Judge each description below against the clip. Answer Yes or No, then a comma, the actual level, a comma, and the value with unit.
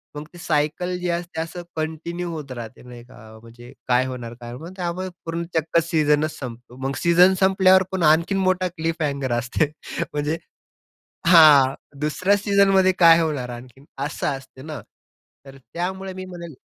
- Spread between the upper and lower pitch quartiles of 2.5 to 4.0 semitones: No, average, 4.9 semitones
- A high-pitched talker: No, medium, 160 Hz